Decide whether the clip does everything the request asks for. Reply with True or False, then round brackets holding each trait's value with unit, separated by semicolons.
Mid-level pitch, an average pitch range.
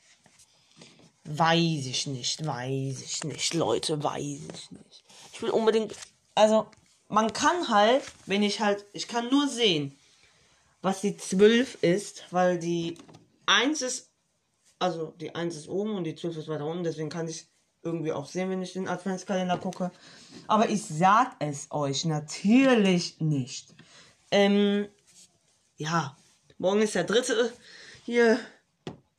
True (180 Hz; 5.0 semitones)